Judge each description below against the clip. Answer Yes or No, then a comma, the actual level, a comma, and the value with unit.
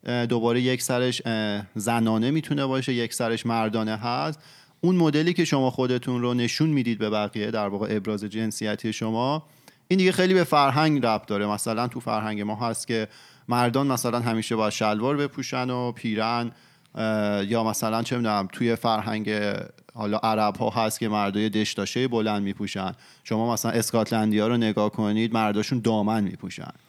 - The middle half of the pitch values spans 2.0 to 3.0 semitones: Yes, average, 2.7 semitones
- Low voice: Yes, low, 115 Hz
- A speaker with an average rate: No, fast, 160 wpm